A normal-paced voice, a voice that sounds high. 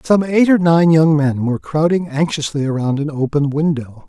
No: average, 190 wpm; medium, 155 Hz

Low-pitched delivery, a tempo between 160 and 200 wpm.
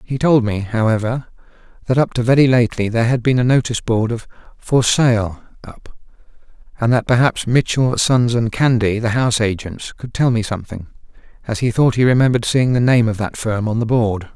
Yes: low, 115 Hz; average, 195 wpm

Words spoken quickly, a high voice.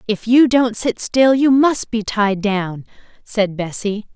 No: average, 175 wpm; high, 225 Hz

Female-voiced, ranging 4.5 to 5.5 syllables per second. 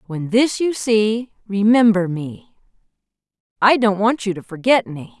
No: female; 4.1 syllables/s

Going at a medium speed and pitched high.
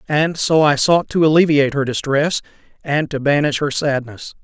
No: average, 175 wpm; medium, 145 Hz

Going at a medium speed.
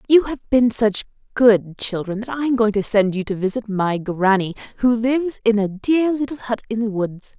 No: fast, 220 wpm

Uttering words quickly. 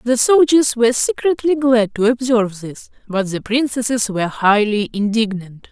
No: average, 145 wpm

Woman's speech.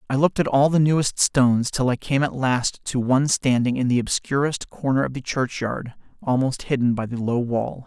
No: male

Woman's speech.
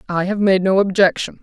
Yes: female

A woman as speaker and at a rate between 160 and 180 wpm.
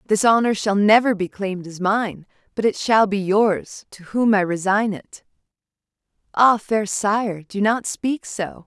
Yes: female; average, 175 wpm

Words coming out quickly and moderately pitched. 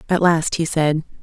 No: average, 195 wpm; medium, 165 Hz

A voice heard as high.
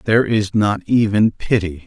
No: low, 105 Hz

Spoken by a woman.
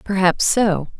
Yes: female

